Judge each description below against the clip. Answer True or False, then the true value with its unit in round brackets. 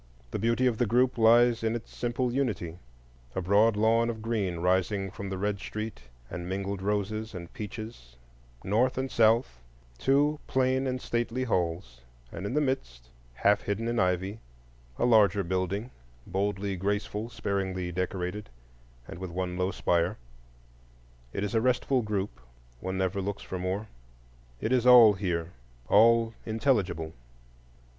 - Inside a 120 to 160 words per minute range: True (145 wpm)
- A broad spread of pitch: False (4.0 semitones)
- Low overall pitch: True (105 Hz)